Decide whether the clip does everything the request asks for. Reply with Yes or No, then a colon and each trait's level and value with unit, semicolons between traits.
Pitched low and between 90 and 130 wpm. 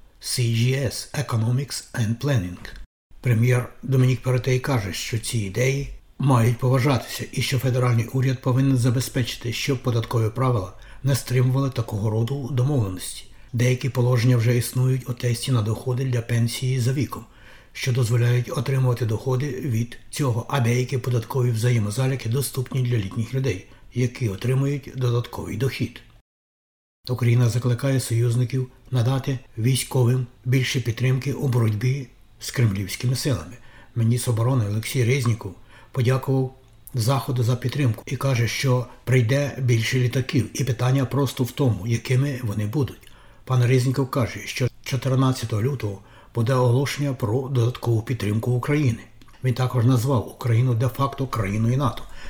Yes: low, 125 Hz; average, 125 wpm